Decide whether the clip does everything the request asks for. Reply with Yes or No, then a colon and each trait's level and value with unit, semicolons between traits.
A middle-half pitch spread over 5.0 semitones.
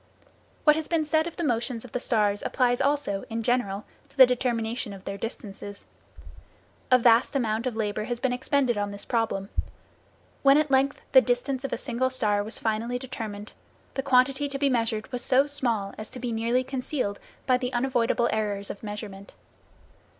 No: average, 3.4 semitones